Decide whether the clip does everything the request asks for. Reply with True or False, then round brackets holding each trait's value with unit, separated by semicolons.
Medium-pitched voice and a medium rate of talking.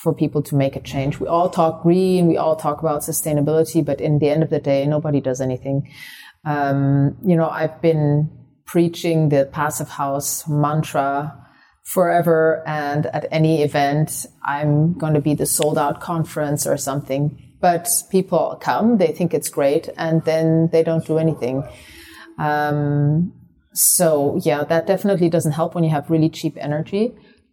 True (155 Hz; 165 wpm)